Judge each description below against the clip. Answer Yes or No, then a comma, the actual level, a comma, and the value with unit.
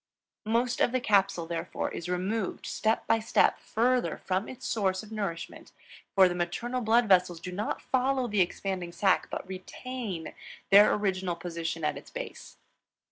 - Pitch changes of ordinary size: Yes, average, 4.2 semitones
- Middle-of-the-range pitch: No, high, 195 Hz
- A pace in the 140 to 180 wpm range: Yes, average, 160 wpm